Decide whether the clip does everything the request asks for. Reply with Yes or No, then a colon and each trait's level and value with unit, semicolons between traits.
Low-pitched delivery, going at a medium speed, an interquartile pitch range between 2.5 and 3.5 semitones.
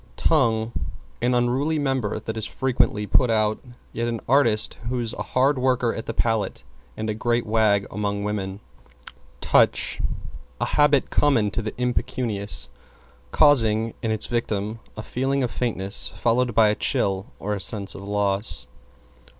Yes: low, 115 Hz; average, 150 wpm; average, 3.1 semitones